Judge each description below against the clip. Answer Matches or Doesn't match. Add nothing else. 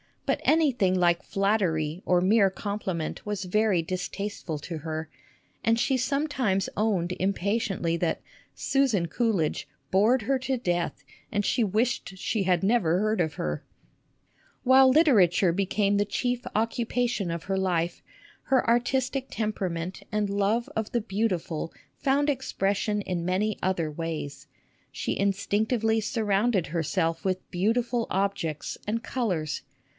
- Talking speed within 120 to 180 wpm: Matches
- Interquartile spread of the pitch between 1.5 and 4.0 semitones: Doesn't match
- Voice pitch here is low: Doesn't match